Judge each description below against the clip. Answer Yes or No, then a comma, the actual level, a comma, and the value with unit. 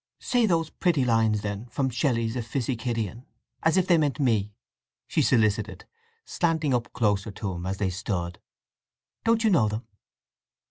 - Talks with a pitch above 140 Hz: No, low, 120 Hz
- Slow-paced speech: No, average, 150 wpm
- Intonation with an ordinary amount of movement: No, wide, 6.1 semitones